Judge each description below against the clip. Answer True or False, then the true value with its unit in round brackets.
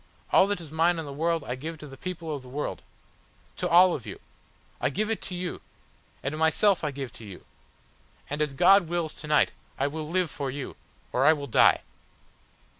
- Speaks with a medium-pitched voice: True (155 Hz)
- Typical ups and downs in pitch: True (3.6 semitones)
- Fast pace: True (210 wpm)